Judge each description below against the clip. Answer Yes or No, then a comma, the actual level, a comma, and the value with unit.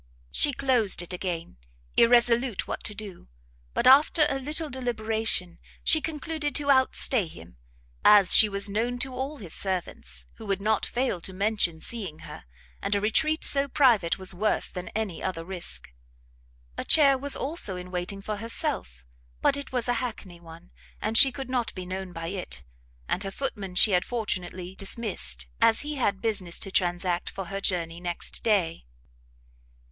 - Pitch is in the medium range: No, high, 205 Hz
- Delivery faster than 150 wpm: Yes, average, 170 wpm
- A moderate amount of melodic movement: No, wide, 5.7 semitones